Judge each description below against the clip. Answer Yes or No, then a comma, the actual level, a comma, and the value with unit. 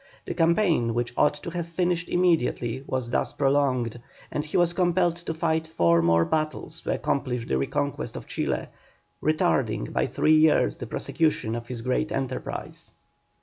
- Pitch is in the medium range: Yes, medium, 150 Hz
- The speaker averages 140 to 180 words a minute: Yes, average, 160 wpm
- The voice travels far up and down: Yes, wide, 5.7 semitones